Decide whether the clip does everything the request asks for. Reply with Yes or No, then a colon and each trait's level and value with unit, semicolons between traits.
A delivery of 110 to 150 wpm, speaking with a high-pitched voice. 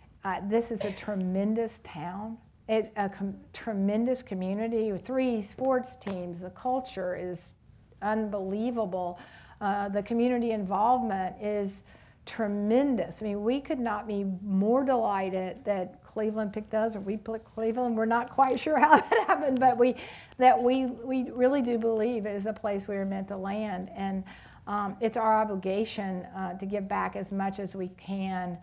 No: average, 165 wpm; high, 210 Hz